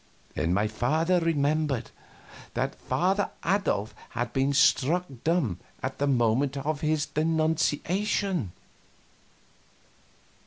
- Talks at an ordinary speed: No, slow, 95 wpm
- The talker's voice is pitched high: No, medium, 150 Hz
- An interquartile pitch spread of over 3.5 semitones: Yes, average, 5.2 semitones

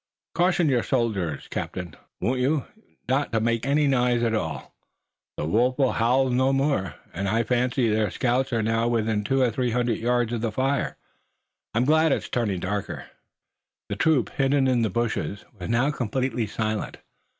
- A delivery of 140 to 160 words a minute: No, average, 170 wpm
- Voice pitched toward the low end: Yes, low, 120 Hz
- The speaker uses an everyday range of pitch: Yes, average, 3.1 semitones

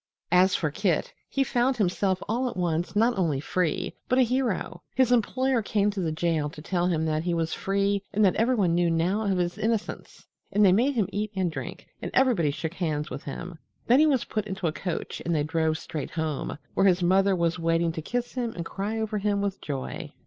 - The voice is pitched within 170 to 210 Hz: Yes, high, 190 Hz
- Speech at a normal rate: No, fast, 220 wpm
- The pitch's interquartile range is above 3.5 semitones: Yes, average, 4.5 semitones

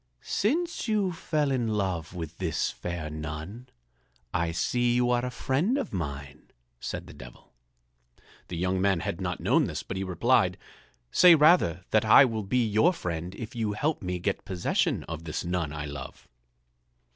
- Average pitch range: No, wide, 7.1 semitones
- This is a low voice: Yes, very low, 95 Hz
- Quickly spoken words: No, average, 170 wpm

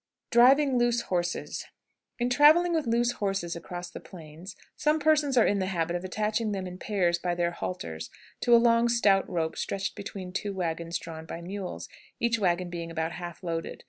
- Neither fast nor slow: Yes, average, 185 wpm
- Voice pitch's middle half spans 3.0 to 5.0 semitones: No, wide, 5.4 semitones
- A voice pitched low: No, high, 190 Hz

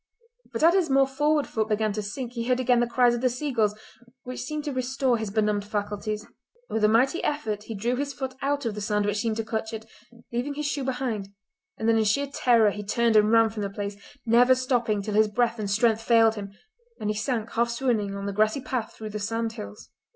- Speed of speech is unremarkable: No, fast, 230 wpm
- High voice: Yes, high, 225 Hz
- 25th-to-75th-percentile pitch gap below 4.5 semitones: Yes, average, 3.2 semitones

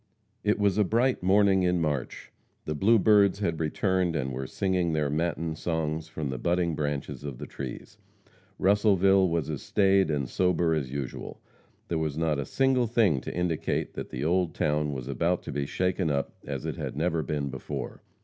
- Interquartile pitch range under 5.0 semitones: Yes, average, 4.4 semitones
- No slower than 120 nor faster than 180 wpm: No, average, 190 wpm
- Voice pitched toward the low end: Yes, very low, 80 Hz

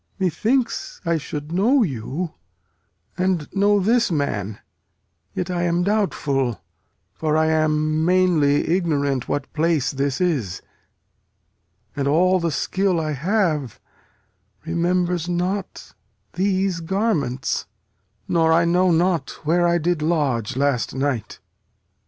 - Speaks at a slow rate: Yes, slow, 115 wpm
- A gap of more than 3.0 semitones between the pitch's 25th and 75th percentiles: Yes, average, 4.1 semitones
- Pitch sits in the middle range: Yes, medium, 165 Hz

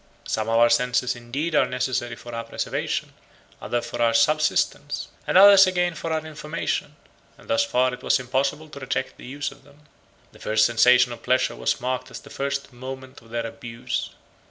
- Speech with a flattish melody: No, average, 3.5 semitones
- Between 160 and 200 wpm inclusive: Yes, average, 195 wpm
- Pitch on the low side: Yes, low, 130 Hz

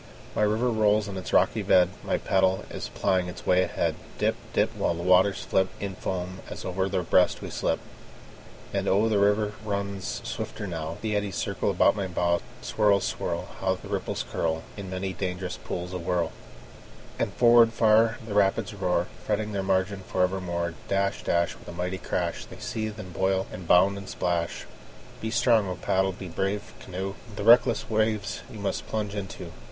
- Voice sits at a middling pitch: No, very low, 95 Hz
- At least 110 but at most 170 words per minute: No, average, 185 wpm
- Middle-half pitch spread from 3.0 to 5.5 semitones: No, narrow, 2.4 semitones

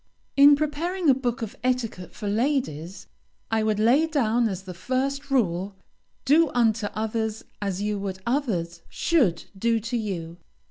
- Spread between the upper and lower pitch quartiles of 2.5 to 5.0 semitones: No, wide, 5.5 semitones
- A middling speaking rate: Yes, average, 150 wpm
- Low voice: No, high, 225 Hz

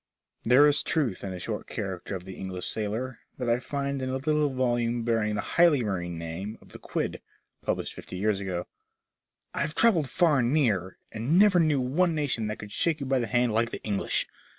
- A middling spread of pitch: No, wide, 5.8 semitones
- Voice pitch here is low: Yes, low, 120 Hz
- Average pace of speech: No, fast, 210 wpm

